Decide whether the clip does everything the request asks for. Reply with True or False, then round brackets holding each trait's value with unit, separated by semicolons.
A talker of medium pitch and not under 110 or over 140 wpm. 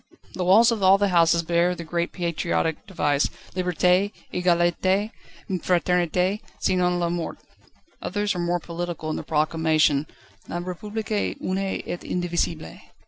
True (175 Hz; 135 wpm)